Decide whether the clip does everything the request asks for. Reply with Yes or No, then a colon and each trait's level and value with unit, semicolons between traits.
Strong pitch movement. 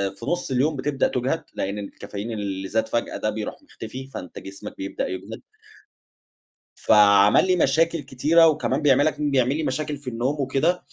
Yes: wide, 6.0 semitones